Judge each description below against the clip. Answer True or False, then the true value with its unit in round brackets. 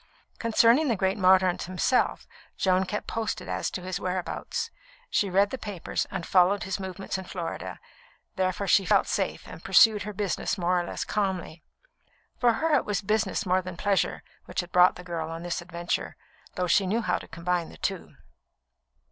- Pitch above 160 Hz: True (185 Hz)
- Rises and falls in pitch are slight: True (2.3 semitones)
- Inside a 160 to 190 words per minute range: True (180 wpm)